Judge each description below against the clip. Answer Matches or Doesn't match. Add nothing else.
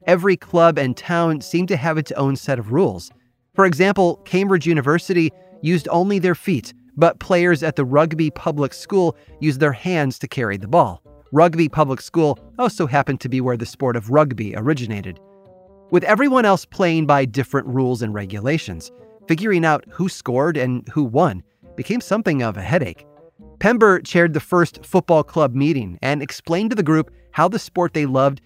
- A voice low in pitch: Doesn't match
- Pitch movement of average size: Matches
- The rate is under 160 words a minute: Doesn't match